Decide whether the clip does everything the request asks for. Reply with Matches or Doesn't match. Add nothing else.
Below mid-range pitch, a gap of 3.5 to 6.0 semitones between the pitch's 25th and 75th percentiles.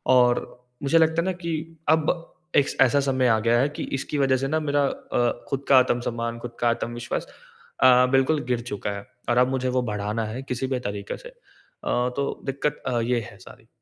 Doesn't match